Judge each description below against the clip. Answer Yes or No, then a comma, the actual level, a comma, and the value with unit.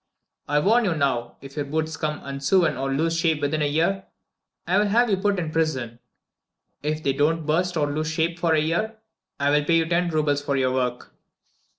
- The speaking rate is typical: No, fast, 210 wpm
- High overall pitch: No, medium, 155 Hz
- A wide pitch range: No, average, 2.9 semitones